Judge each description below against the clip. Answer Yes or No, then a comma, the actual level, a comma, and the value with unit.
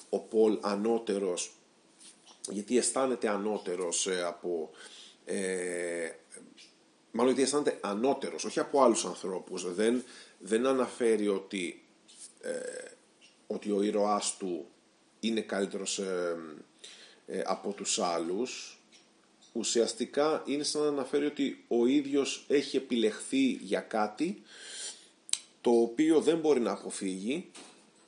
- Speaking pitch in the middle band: No, low, 115 Hz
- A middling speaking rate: No, slow, 105 wpm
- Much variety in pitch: Yes, wide, 6.3 semitones